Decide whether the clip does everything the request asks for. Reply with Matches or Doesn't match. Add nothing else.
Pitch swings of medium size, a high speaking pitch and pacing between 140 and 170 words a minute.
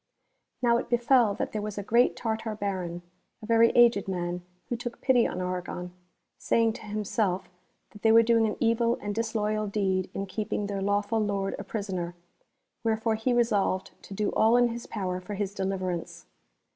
Doesn't match